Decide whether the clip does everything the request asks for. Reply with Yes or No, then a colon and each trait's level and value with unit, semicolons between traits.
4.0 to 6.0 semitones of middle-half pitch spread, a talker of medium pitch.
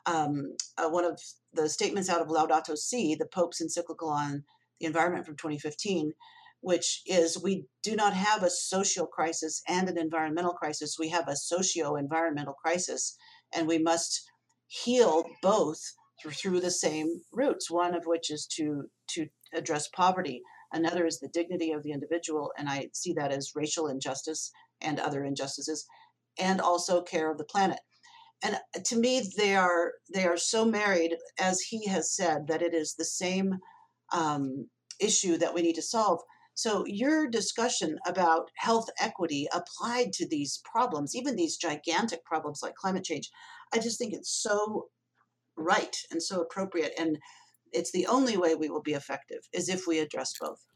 No: average, 3.5 semitones; medium, 170 Hz